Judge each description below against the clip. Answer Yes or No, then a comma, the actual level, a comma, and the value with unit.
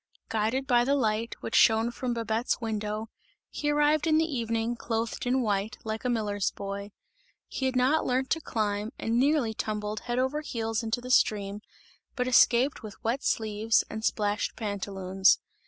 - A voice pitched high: Yes, high, 225 Hz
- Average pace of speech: Yes, average, 170 wpm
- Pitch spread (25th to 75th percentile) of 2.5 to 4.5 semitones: Yes, average, 3.0 semitones